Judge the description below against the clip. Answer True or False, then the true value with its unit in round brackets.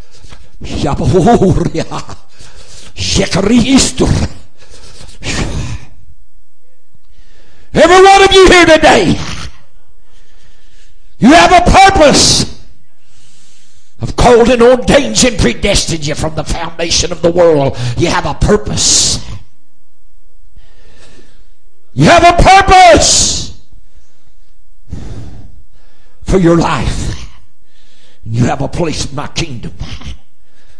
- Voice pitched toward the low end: False (175 Hz)